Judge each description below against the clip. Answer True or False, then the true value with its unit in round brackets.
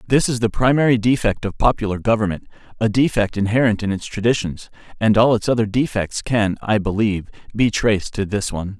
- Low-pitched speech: True (110 Hz)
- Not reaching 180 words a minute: False (185 wpm)